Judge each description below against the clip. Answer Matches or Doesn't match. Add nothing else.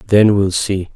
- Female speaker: Doesn't match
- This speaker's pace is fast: Doesn't match